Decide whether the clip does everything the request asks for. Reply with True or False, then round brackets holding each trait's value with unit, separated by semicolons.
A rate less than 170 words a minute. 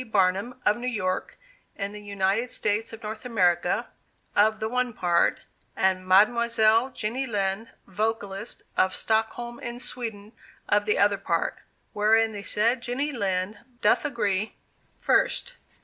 True (135 wpm)